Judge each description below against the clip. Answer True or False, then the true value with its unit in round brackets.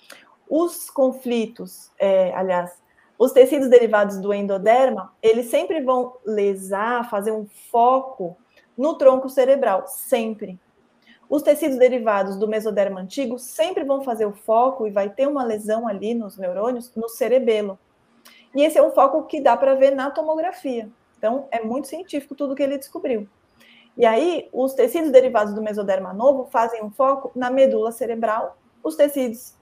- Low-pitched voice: False (245 Hz)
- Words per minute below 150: False (155 wpm)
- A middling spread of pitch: True (4.3 semitones)